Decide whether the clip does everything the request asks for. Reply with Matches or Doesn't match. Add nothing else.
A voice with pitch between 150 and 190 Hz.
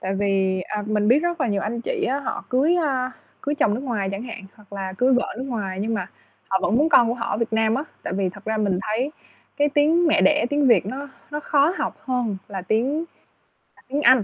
Doesn't match